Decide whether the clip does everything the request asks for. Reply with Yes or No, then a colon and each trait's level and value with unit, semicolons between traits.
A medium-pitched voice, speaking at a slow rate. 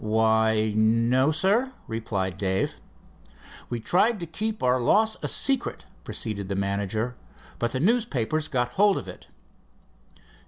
No: low, 120 Hz; slow, 130 wpm